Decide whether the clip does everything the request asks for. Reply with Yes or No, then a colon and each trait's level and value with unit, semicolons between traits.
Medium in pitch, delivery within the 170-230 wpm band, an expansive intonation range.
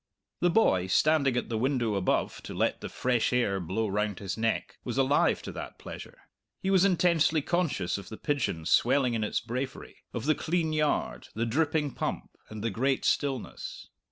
No: low, 125 Hz; average, 185 wpm; wide, 5.9 semitones